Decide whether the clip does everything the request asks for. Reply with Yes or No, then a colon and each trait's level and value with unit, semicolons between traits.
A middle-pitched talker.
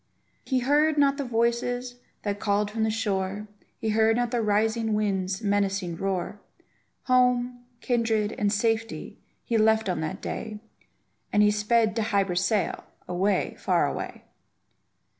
No: high, 220 Hz